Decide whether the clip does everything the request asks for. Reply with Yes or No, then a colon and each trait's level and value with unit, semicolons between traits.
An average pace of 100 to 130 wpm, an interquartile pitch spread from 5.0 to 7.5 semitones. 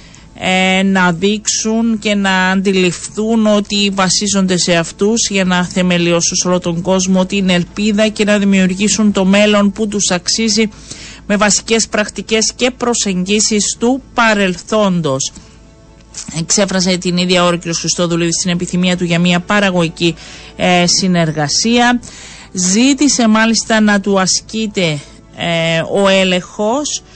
No: average, 120 wpm; average, 3.2 semitones